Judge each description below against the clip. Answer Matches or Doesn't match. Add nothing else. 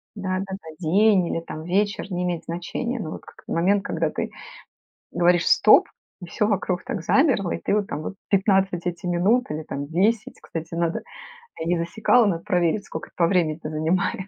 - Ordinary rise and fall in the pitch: Matches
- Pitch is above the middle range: Doesn't match